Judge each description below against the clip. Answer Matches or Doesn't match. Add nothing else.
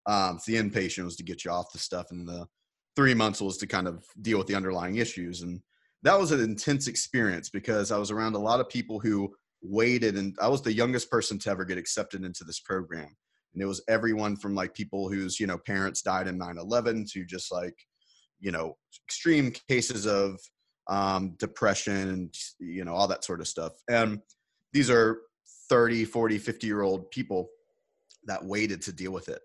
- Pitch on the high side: Doesn't match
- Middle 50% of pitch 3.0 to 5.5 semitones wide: Matches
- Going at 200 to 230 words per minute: Matches